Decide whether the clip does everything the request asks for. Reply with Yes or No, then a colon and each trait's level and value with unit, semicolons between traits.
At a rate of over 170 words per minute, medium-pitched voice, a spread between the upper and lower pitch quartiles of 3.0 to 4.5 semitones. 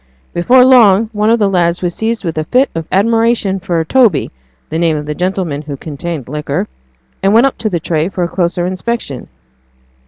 No: fast, 205 wpm; medium, 180 Hz; wide, 5.4 semitones